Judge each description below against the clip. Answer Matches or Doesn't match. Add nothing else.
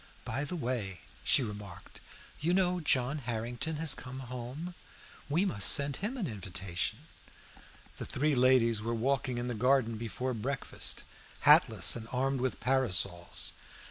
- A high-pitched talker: Doesn't match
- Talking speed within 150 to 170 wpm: Doesn't match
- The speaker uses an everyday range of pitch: Matches